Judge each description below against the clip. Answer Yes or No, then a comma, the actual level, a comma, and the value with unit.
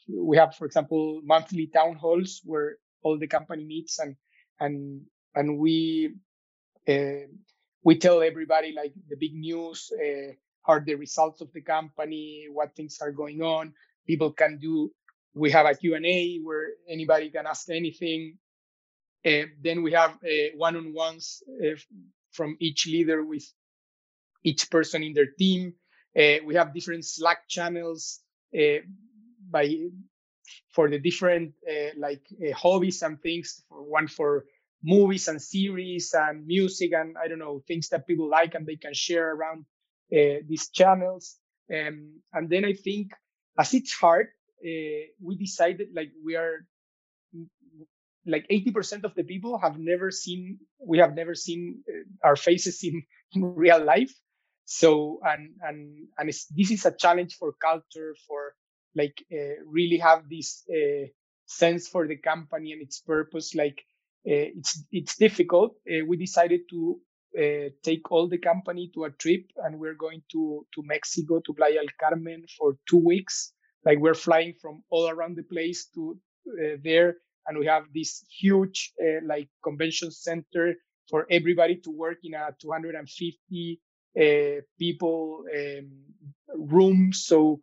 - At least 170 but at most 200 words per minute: No, average, 155 wpm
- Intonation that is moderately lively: No, narrow, 2.2 semitones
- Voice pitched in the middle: Yes, medium, 165 Hz